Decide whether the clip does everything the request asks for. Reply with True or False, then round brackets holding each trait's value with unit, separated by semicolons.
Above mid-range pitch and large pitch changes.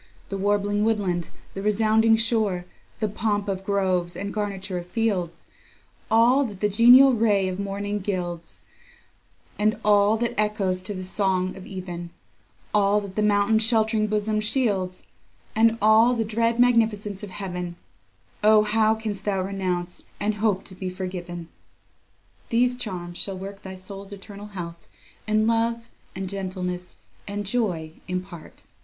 False (205 Hz; 2.7 semitones)